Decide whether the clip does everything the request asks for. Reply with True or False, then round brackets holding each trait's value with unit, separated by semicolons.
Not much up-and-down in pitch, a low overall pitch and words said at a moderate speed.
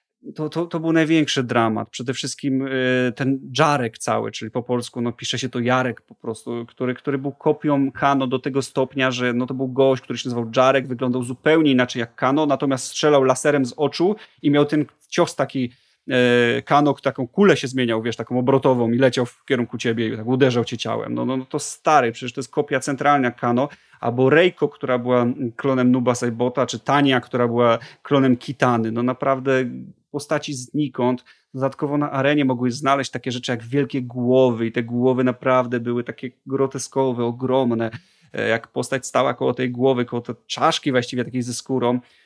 False (2.1 semitones; 130 Hz; 185 wpm)